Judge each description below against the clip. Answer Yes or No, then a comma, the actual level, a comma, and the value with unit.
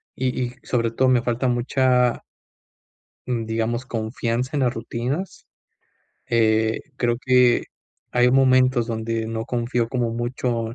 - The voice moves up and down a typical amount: No, narrow, 1.8 semitones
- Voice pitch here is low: Yes, low, 120 Hz